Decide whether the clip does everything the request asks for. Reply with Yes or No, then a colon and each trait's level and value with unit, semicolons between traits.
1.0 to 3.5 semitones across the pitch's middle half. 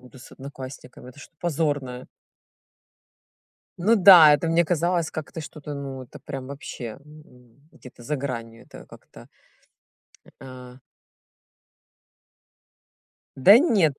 No: average, 4.3 semitones